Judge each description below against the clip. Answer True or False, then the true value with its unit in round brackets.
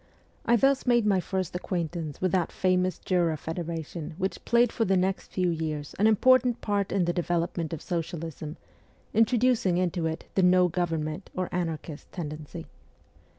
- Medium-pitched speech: True (180 Hz)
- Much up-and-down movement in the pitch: False (3.0 semitones)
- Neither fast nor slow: True (155 wpm)